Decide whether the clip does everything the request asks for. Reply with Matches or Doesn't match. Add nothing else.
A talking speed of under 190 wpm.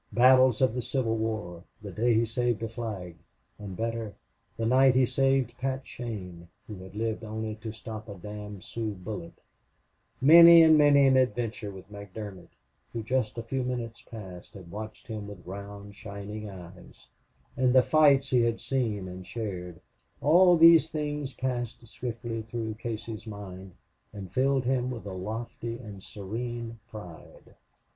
Matches